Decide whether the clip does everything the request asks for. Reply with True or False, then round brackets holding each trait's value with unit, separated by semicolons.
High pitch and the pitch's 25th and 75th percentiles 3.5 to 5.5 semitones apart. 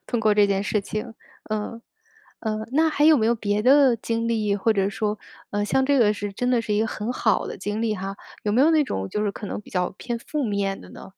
False (215 Hz; 2.7 semitones)